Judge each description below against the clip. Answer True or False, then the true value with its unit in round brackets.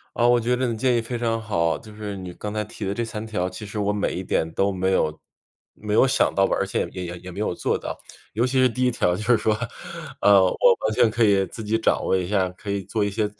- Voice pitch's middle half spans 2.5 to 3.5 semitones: True (3.0 semitones)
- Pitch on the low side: True (105 Hz)